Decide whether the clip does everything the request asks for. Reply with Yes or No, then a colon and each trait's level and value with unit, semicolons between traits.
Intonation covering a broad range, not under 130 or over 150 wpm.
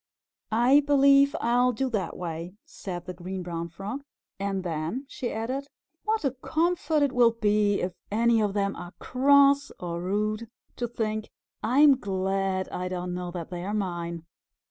No: wide, 6.0 semitones; average, 165 wpm